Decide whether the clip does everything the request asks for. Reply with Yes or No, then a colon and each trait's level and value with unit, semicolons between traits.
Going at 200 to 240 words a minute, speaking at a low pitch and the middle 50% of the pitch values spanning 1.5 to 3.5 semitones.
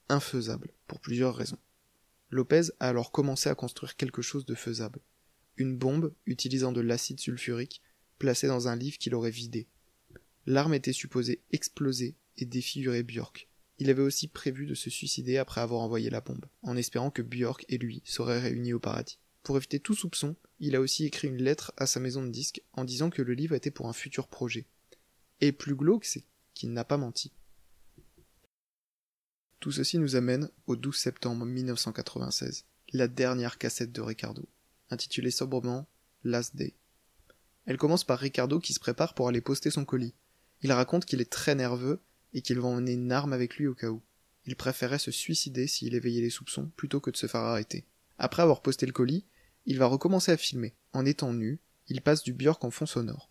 No: average, 190 wpm; low, 130 Hz; average, 2.7 semitones